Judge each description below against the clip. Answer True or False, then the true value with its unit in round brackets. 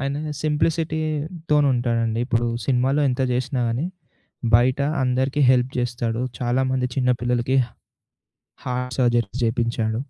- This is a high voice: False (125 Hz)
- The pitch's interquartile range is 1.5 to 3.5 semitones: True (2.5 semitones)